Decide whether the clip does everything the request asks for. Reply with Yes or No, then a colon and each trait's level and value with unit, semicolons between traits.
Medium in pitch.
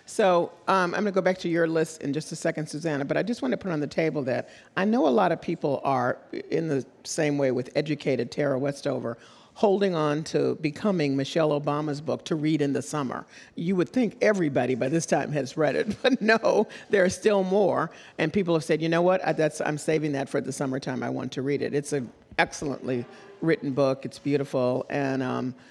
Yes: medium, 150 Hz